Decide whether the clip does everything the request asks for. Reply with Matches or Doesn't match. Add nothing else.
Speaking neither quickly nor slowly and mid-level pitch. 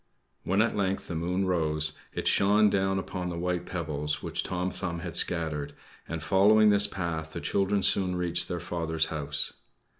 Doesn't match